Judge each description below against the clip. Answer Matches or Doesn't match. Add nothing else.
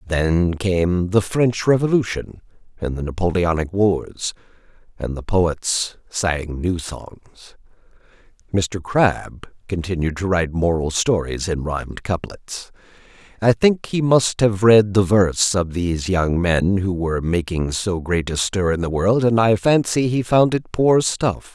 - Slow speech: Doesn't match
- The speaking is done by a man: Matches